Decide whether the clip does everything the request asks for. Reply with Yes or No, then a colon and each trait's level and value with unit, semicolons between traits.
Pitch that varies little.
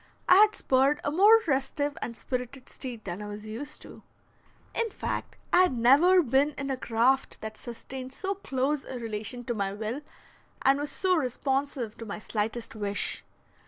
No: average, 4.3 semitones